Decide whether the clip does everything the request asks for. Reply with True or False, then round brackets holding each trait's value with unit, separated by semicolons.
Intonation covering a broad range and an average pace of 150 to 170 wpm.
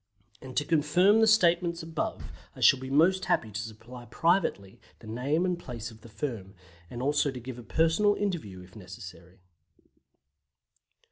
True (7.5 semitones; 160 wpm)